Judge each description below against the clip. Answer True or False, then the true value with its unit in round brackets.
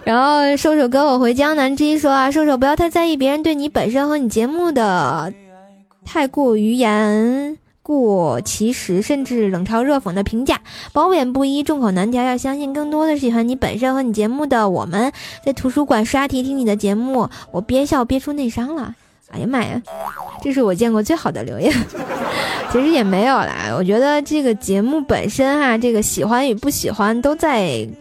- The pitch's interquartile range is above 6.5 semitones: False (5.1 semitones)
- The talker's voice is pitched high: True (255 Hz)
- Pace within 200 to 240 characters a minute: False (285 characters per minute)